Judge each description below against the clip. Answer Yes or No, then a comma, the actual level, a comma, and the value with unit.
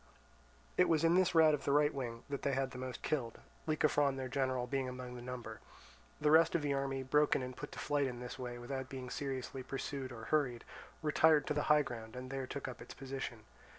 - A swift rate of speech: Yes, fast, 225 wpm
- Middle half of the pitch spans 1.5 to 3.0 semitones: Yes, average, 2.7 semitones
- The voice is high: No, low, 135 Hz